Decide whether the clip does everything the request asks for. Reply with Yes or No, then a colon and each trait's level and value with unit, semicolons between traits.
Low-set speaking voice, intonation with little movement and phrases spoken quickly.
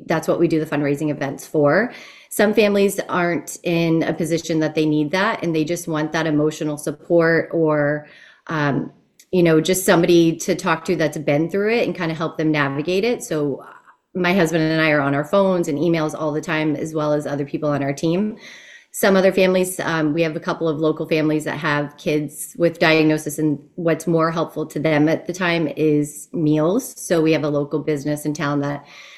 No: medium, 160 Hz; narrow, 2.3 semitones; fast, 210 wpm